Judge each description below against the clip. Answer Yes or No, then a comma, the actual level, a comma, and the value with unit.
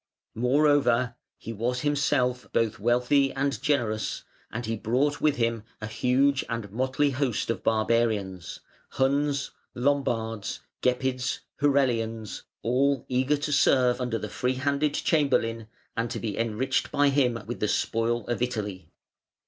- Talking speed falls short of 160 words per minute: Yes, slow, 135 wpm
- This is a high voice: No, low, 125 Hz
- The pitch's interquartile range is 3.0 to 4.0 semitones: Yes, average, 3.4 semitones